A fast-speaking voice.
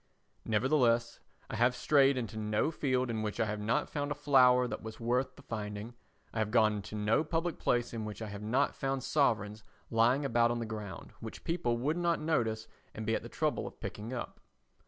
Yes: fast, 210 wpm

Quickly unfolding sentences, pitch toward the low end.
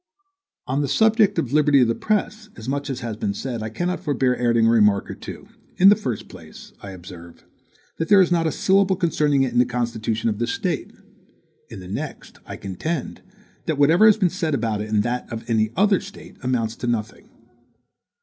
Yes: fast, 210 wpm; low, 125 Hz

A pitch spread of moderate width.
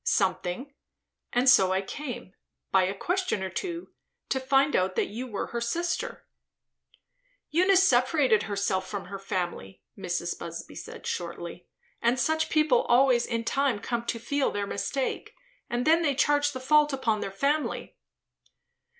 No: wide, 6.5 semitones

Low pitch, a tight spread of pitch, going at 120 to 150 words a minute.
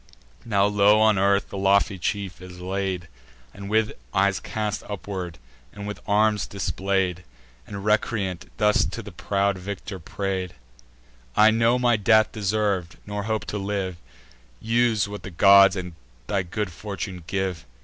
Yes: low, 100 Hz; narrow, 1.9 semitones; average, 145 wpm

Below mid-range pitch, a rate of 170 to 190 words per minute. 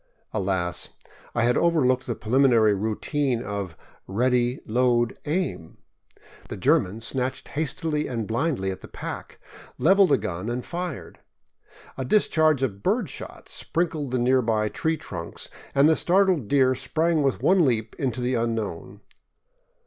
No: low, 125 Hz; average, 140 wpm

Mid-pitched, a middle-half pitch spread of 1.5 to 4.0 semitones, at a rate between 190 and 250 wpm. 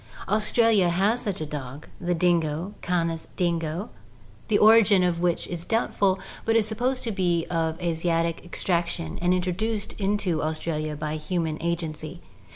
No: medium, 175 Hz; average, 3.6 semitones; average, 160 wpm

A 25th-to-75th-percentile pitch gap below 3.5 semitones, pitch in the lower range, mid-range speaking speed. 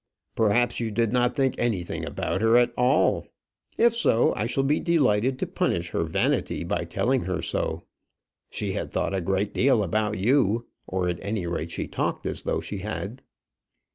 No: average, 4.4 semitones; low, 110 Hz; average, 180 wpm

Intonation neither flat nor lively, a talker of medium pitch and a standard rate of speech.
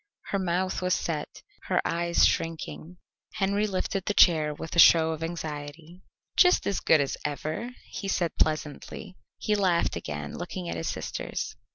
Yes: average, 3.6 semitones; medium, 170 Hz; average, 160 wpm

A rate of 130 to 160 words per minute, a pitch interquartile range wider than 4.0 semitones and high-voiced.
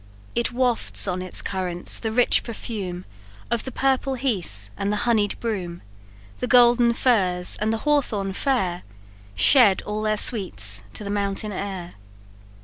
Yes: average, 145 wpm; average, 4.4 semitones; high, 210 Hz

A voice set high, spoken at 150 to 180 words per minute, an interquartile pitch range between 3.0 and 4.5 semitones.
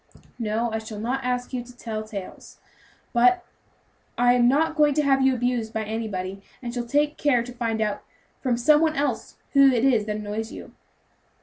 No: high, 240 Hz; average, 195 wpm; average, 3.5 semitones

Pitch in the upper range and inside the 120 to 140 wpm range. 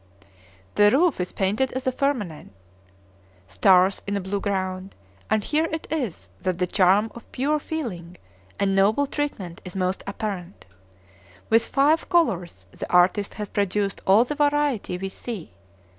No: high, 200 Hz; average, 150 wpm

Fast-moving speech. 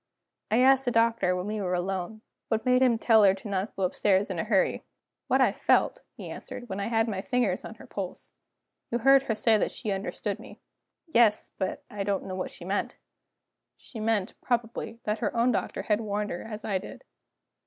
Yes: fast, 210 wpm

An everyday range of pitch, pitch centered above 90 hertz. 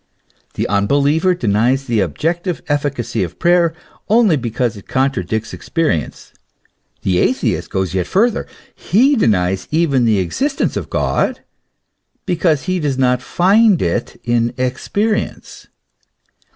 No: wide, 8.0 semitones; low, 135 Hz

